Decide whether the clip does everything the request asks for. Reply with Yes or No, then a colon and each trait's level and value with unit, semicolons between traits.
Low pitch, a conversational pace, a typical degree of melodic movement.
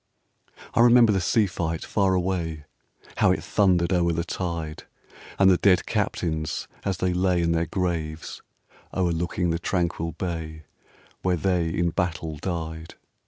No: very low, 85 Hz; average, 145 wpm; narrow, 2.1 semitones